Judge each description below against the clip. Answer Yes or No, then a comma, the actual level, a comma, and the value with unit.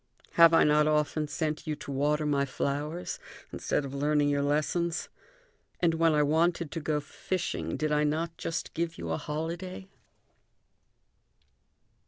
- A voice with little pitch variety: Yes, narrow, 2.1 semitones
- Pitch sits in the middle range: Yes, medium, 150 Hz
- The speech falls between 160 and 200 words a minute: No, average, 150 wpm